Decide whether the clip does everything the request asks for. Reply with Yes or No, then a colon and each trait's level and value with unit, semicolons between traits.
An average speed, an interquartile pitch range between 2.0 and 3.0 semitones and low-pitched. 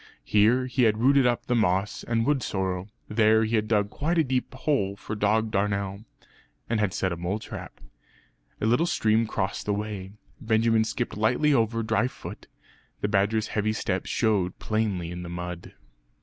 Yes: average, 175 wpm; narrow, 2.6 semitones; low, 110 Hz